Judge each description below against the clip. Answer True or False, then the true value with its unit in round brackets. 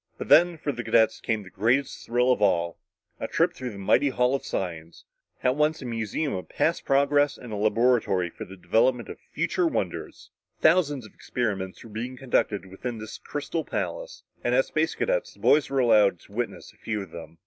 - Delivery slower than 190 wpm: False (205 wpm)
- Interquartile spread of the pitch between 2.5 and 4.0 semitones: False (5.3 semitones)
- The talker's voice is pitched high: False (120 Hz)